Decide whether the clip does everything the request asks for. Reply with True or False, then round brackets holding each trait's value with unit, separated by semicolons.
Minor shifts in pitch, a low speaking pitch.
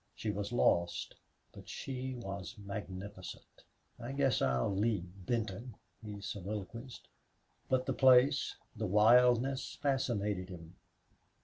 False (4.3 semitones; 110 Hz)